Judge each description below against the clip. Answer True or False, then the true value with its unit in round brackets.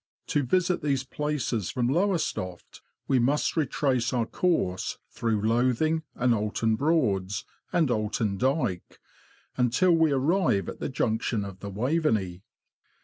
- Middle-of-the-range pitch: False (125 Hz)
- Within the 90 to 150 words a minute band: True (135 wpm)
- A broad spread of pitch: True (6.0 semitones)